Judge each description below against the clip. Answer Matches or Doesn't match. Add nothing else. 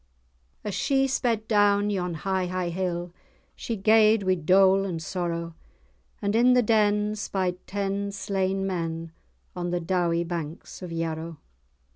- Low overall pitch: Doesn't match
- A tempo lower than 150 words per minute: Matches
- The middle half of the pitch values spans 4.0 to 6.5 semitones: Doesn't match